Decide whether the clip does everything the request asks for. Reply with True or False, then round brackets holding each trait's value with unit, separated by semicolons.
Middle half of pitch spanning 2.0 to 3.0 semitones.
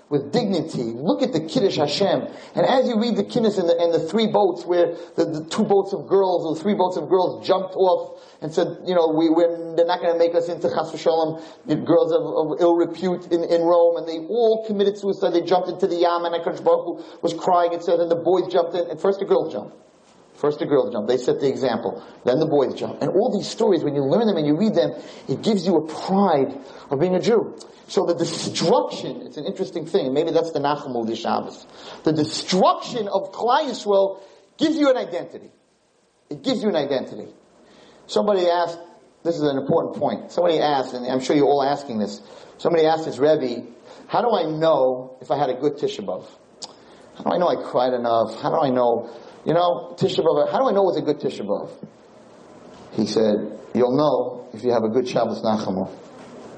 False (4.1 semitones)